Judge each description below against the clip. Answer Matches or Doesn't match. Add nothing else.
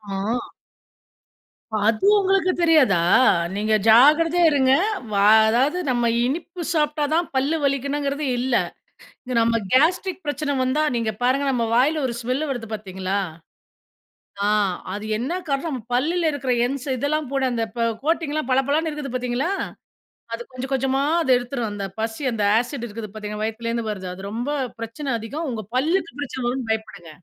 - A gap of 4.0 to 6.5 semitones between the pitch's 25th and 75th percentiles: Matches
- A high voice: Matches